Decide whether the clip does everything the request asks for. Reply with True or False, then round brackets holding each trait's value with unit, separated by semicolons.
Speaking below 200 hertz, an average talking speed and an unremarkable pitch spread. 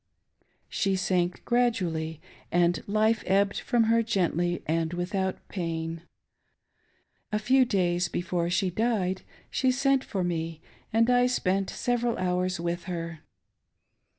False (185 Hz; 125 wpm; 4.4 semitones)